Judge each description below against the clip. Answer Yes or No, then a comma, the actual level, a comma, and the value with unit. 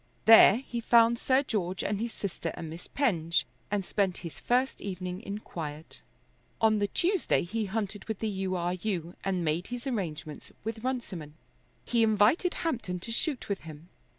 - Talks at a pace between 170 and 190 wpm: Yes, average, 175 wpm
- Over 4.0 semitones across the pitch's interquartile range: Yes, average, 4.7 semitones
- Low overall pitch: No, high, 205 Hz